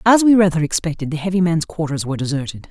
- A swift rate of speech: Yes, fast, 220 wpm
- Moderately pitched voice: Yes, medium, 165 Hz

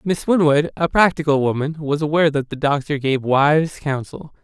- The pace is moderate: Yes, average, 175 wpm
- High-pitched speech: No, medium, 150 Hz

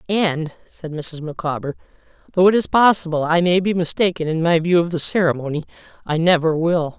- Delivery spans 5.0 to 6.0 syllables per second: Yes, 5.4 syllables/s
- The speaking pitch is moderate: Yes, medium, 170 Hz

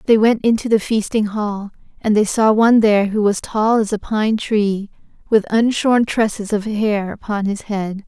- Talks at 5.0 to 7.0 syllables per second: No, 4.6 syllables/s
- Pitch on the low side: No, high, 215 Hz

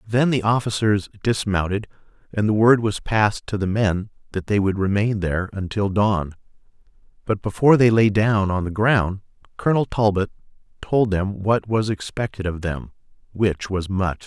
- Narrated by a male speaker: Yes, male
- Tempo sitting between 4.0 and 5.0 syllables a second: Yes, 4.9 syllables/s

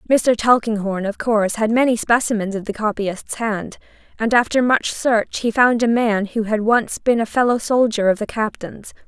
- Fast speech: No, average, 190 wpm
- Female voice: Yes, female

